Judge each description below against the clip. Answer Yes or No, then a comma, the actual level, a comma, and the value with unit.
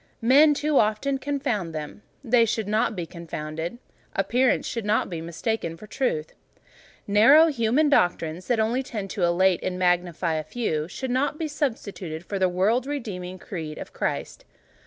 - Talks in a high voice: Yes, high, 210 Hz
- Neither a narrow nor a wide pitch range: No, wide, 6.5 semitones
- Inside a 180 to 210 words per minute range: No, average, 160 wpm